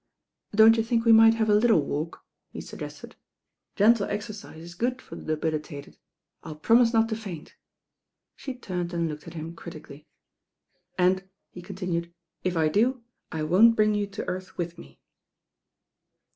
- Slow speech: No, average, 165 wpm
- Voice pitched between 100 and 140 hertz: No, medium, 185 Hz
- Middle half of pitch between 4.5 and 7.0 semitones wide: Yes, average, 5.2 semitones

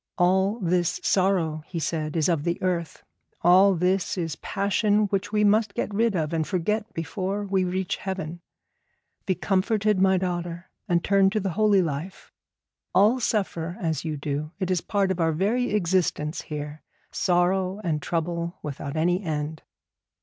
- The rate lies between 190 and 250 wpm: No, average, 160 wpm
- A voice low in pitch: No, medium, 180 Hz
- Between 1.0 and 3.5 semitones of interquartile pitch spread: Yes, average, 3.2 semitones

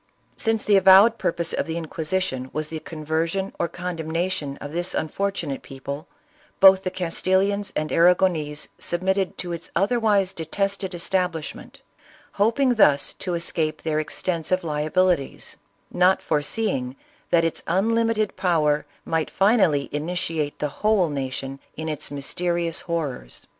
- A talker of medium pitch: Yes, medium, 170 Hz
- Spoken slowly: Yes, slow, 130 wpm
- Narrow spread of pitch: No, average, 3.7 semitones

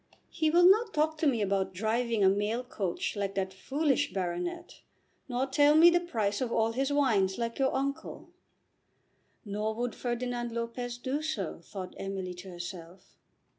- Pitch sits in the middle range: No, high, 230 Hz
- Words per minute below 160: No, average, 165 wpm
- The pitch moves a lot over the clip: Yes, wide, 5.8 semitones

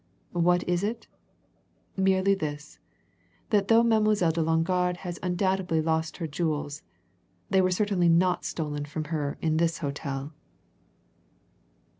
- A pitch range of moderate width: Yes, average, 3.3 semitones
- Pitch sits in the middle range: Yes, medium, 170 Hz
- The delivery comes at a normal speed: No, slow, 125 wpm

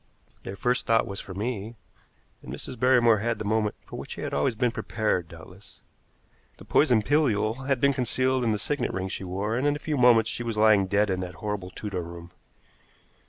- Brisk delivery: Yes, fast, 210 wpm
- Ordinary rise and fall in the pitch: Yes, average, 4.0 semitones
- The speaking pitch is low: Yes, low, 110 Hz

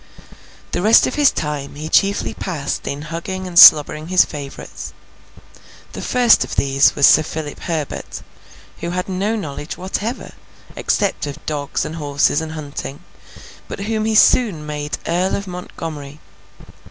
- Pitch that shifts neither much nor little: Yes, average, 4.4 semitones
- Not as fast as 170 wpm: Yes, average, 150 wpm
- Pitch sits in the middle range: Yes, medium, 160 Hz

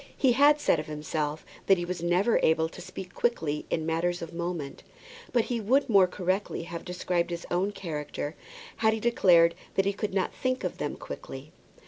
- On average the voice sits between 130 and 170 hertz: No, medium, 180 Hz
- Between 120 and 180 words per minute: No, average, 190 wpm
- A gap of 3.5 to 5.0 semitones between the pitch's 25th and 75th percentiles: Yes, average, 3.8 semitones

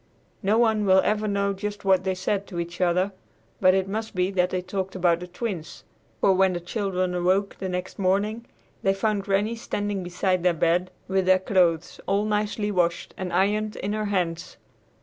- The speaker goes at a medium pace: Yes, average, 190 wpm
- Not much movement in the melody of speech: Yes, narrow, 2.2 semitones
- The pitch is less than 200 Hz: Yes, high, 190 Hz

